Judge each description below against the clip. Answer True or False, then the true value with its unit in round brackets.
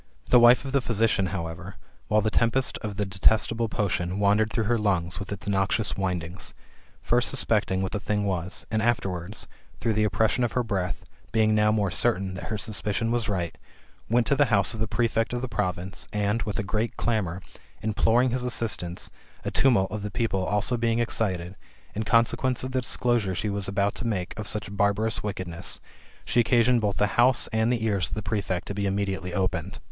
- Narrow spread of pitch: False (3.1 semitones)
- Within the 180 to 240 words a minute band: True (200 wpm)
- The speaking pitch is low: True (105 Hz)